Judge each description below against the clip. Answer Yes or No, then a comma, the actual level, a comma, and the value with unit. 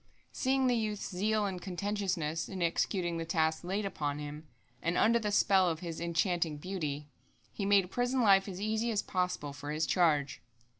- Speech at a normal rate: Yes, average, 180 wpm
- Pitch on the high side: No, medium, 180 Hz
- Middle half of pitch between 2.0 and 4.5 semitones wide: Yes, average, 4.1 semitones